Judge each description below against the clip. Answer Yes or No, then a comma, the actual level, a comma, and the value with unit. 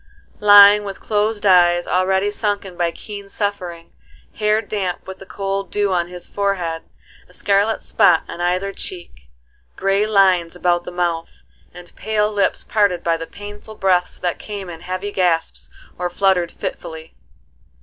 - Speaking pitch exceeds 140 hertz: Yes, high, 190 Hz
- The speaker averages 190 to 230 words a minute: No, average, 150 wpm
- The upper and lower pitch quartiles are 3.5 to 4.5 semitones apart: No, narrow, 2.6 semitones